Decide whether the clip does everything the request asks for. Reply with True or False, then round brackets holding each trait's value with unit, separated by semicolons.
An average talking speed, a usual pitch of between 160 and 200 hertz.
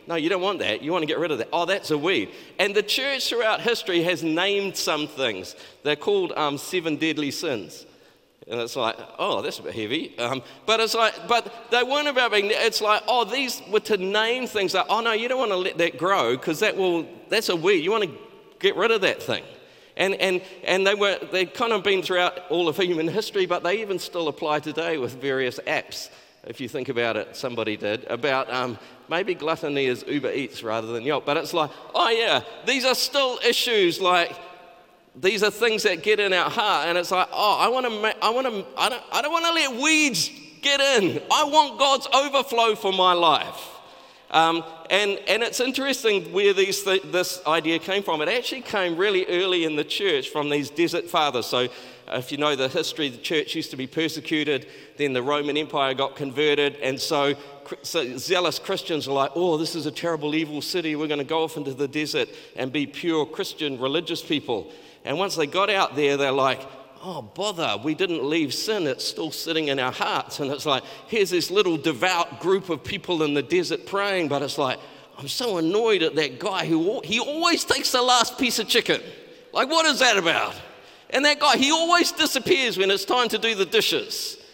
False (215 wpm; 185 Hz)